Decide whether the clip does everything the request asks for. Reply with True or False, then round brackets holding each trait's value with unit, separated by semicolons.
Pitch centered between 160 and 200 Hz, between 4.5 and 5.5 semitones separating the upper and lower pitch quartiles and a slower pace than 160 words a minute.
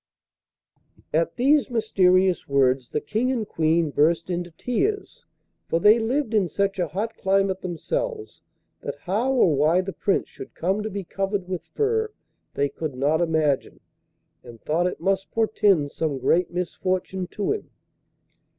True (185 Hz; 5.1 semitones; 150 wpm)